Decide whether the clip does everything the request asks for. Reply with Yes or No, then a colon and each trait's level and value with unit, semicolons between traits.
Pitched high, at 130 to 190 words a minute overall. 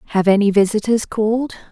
Yes: high, 215 Hz; average, 140 wpm